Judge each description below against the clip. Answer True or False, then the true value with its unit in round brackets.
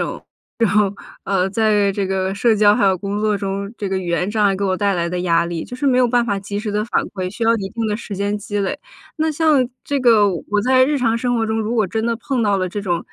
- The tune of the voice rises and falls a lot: False (3.1 semitones)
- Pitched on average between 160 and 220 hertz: True (205 Hz)